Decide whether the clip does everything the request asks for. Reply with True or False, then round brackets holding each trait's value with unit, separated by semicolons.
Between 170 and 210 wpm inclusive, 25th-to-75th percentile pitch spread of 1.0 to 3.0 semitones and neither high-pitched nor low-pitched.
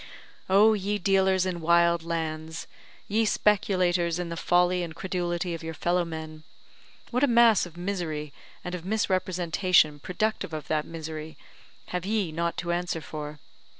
False (150 wpm; 2.7 semitones; 175 Hz)